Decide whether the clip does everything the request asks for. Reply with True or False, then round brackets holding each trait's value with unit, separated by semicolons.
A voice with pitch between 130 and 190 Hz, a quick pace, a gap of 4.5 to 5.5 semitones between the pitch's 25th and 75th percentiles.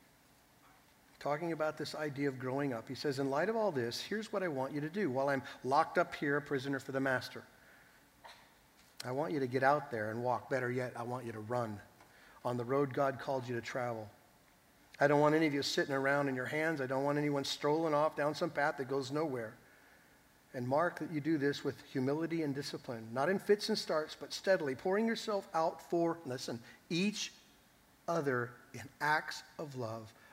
False (140 Hz; 210 wpm; 3.9 semitones)